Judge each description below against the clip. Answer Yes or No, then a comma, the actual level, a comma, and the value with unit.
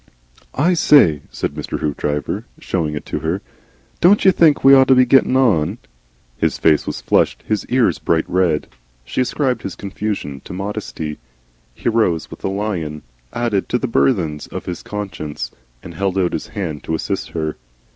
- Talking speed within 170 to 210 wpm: Yes, average, 175 wpm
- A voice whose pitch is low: Yes, very low, 95 Hz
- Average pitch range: No, wide, 7.4 semitones